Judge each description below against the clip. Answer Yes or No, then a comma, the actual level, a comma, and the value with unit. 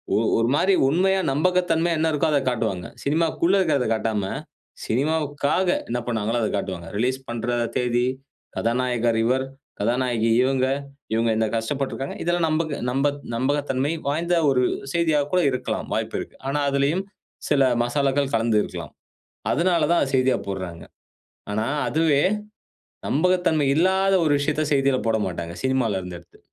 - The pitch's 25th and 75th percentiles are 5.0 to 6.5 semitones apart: Yes, wide, 5.5 semitones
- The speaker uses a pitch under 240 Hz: Yes, low, 135 Hz